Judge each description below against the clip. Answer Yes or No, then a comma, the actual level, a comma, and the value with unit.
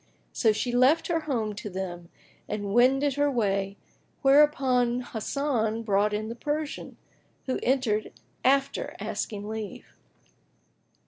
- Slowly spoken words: Yes, slow, 120 wpm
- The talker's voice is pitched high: Yes, high, 240 Hz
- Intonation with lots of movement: No, average, 4.5 semitones